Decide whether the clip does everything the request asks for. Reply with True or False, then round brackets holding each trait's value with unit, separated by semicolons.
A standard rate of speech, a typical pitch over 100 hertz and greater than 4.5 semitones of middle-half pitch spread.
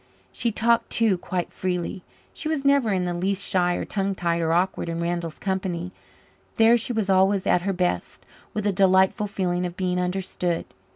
False (185 wpm; 185 Hz; 2.4 semitones)